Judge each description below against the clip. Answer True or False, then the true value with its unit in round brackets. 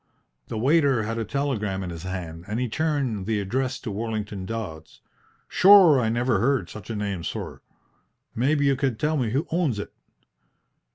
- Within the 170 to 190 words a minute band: True (175 wpm)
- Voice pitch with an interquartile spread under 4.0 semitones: False (5.2 semitones)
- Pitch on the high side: False (115 Hz)